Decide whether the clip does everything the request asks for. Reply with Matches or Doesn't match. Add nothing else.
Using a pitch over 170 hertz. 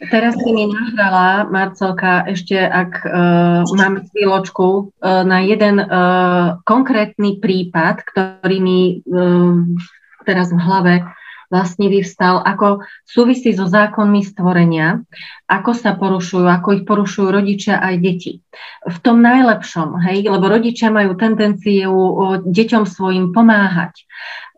Matches